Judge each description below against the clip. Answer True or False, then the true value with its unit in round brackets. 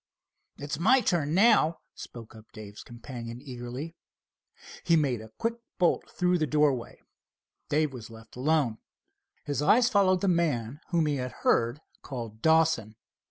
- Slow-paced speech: False (145 wpm)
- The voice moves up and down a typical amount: False (5.9 semitones)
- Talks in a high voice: False (145 Hz)